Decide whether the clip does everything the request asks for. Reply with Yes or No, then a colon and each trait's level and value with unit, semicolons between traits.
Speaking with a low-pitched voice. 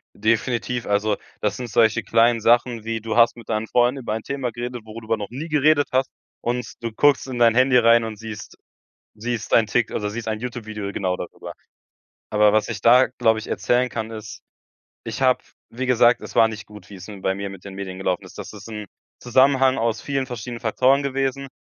Yes: low, 115 Hz